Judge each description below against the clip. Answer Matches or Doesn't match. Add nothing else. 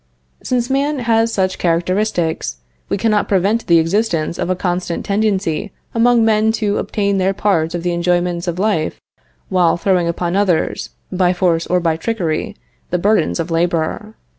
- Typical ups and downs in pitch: Matches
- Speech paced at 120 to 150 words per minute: Doesn't match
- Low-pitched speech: Doesn't match